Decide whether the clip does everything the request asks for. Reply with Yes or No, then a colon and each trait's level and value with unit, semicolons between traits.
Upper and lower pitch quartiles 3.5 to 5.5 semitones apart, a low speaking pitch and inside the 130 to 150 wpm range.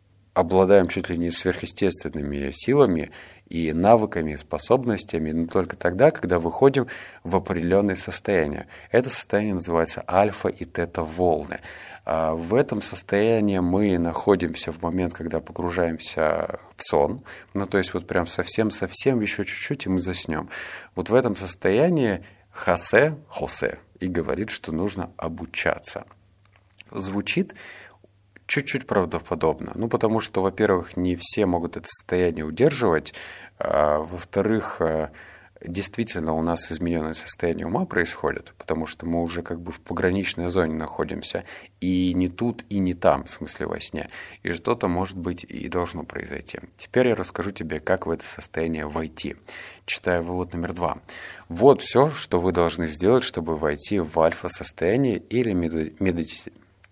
No: average, 3.0 semitones; very low, 90 Hz; average, 140 wpm